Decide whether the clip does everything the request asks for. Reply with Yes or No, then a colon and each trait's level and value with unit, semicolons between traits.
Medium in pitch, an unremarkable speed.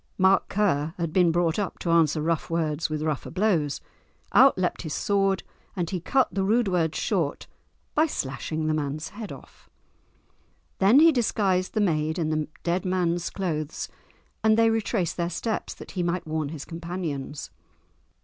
Yes: medium, 175 Hz; average, 170 wpm